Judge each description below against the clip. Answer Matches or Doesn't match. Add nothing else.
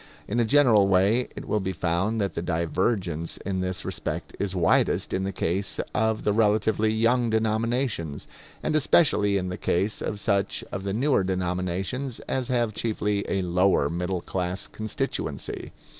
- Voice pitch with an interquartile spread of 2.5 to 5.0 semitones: Matches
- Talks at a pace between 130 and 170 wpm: Matches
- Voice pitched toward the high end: Doesn't match